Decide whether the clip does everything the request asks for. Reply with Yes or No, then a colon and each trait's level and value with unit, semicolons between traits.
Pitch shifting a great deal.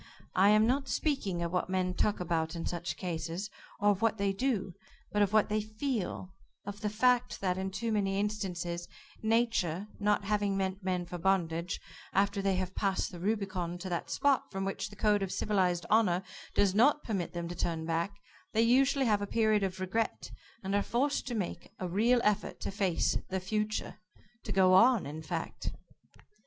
No: average, 2.9 semitones